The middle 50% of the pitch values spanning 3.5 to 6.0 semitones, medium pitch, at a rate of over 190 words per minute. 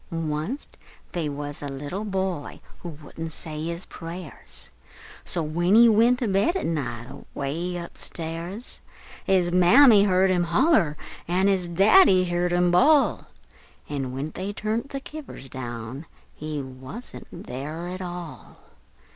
No: average, 4.3 semitones; medium, 175 Hz; average, 140 wpm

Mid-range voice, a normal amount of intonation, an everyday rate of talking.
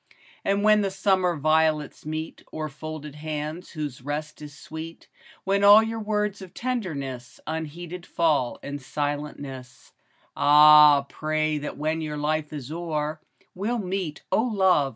Yes: medium, 155 Hz; average, 3.8 semitones; average, 145 wpm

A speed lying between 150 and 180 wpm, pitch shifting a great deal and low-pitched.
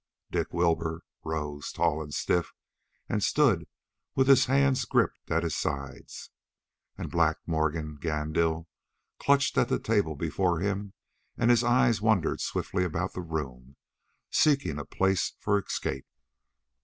No: slow, 135 wpm; wide, 5.7 semitones; very low, 85 Hz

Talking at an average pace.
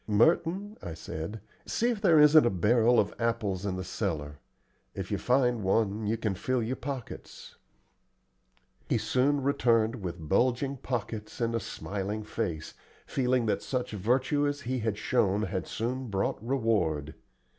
Yes: average, 155 wpm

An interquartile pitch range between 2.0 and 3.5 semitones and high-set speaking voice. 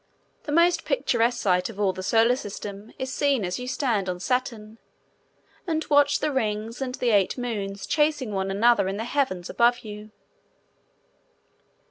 No: average, 4.5 semitones; high, 230 Hz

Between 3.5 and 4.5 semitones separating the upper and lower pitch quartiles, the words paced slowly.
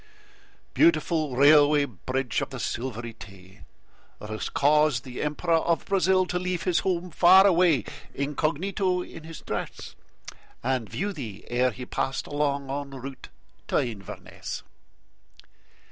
No: average, 5.3 semitones; slow, 130 wpm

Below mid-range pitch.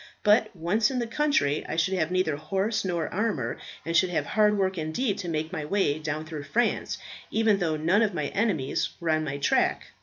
No: medium, 175 Hz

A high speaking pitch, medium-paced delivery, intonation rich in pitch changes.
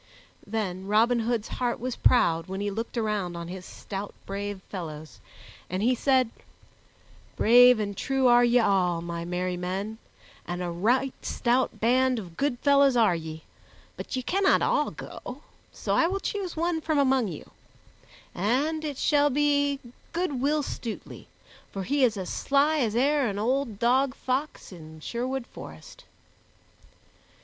Yes: high, 235 Hz; average, 155 wpm; wide, 5.9 semitones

